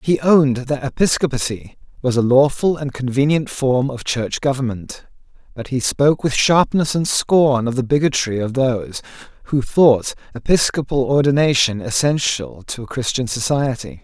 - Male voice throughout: Yes, male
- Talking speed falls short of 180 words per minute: Yes, average, 145 wpm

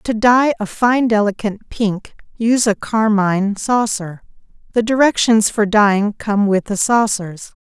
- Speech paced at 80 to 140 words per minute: Yes, slow, 135 wpm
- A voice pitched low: No, high, 215 Hz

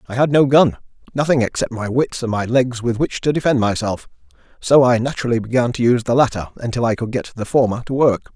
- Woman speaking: No, male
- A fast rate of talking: Yes, fast, 230 wpm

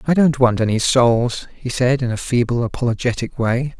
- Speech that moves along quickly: No, average, 190 wpm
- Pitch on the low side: Yes, low, 125 Hz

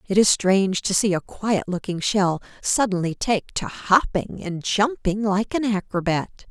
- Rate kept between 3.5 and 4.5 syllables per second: Yes, 4.4 syllables/s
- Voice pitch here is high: Yes, high, 200 Hz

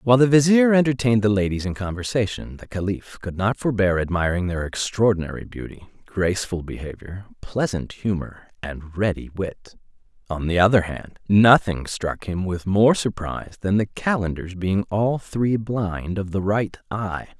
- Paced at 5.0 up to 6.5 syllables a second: No, 4.8 syllables/s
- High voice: No, low, 100 Hz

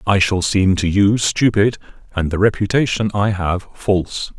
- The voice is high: No, low, 100 Hz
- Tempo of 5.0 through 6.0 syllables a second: No, 4.4 syllables/s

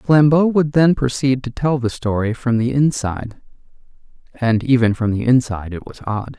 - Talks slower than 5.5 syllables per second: Yes, 5.0 syllables/s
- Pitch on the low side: Yes, low, 125 Hz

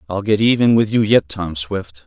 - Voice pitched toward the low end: Yes, low, 100 Hz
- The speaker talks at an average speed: No, fast, 235 wpm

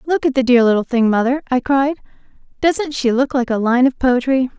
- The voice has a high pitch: Yes, very high, 260 Hz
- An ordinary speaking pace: No, fast, 225 wpm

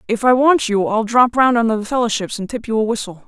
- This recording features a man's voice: No, female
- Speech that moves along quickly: Yes, fast, 275 wpm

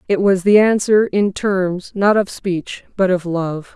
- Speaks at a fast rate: No, average, 190 wpm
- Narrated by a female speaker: Yes, female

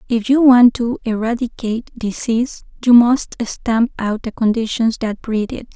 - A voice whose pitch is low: No, high, 230 Hz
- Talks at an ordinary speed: Yes, average, 155 wpm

